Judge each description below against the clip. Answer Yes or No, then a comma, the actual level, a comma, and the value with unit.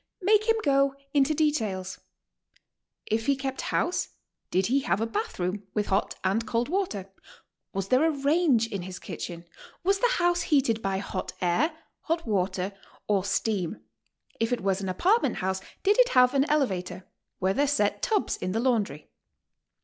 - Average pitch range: No, wide, 7.7 semitones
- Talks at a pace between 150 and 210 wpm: Yes, average, 170 wpm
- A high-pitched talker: Yes, high, 230 Hz